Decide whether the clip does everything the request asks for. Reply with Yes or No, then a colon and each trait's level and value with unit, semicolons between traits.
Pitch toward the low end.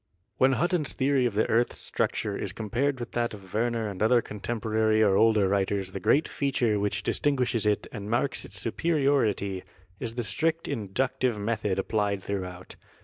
Yes: low, 110 Hz